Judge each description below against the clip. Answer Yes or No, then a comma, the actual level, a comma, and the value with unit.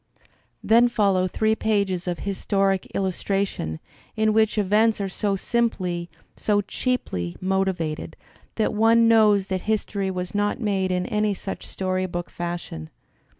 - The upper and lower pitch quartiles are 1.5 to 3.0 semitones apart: Yes, average, 2.7 semitones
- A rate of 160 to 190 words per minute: No, slow, 135 wpm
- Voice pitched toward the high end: Yes, high, 195 Hz